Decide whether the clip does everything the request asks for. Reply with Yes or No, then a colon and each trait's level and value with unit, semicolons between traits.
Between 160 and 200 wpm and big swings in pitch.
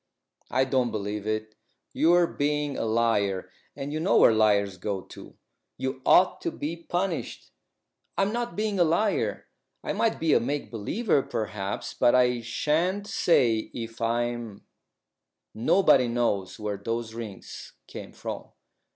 No: average, 145 wpm; wide, 6.9 semitones